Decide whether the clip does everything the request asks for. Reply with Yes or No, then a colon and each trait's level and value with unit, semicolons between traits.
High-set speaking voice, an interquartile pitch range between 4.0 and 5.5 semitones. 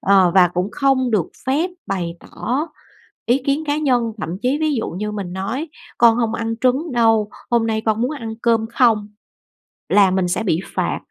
Yes: high, 225 Hz; average, 4.6 semitones